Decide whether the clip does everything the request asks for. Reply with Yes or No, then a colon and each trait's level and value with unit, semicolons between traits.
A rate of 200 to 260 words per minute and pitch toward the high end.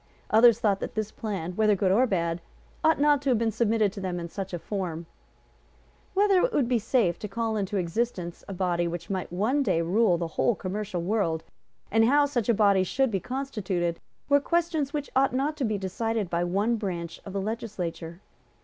Yes: fast, 205 wpm; high, 210 Hz